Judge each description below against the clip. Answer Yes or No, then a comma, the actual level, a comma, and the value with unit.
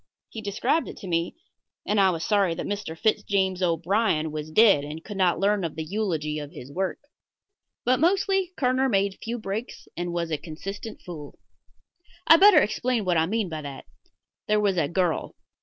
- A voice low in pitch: No, high, 190 Hz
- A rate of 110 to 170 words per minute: No, average, 190 wpm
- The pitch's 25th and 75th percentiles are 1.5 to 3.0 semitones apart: No, average, 5.0 semitones